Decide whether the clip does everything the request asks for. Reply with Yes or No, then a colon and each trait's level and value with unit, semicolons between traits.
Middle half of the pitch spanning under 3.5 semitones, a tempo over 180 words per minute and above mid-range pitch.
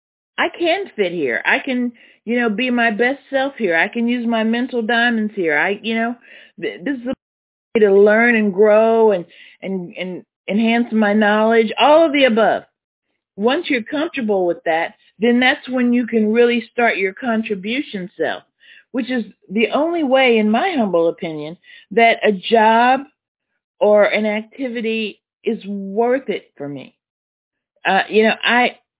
No: average, 2.8 semitones; average, 165 wpm; high, 230 Hz